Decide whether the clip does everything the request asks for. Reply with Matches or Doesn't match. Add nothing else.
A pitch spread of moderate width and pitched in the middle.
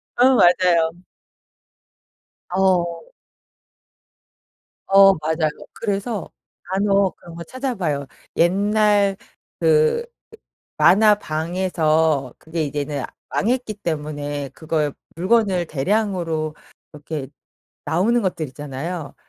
Matches